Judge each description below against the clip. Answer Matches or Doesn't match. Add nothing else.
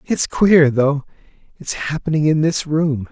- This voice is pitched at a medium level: Matches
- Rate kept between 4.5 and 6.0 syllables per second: Doesn't match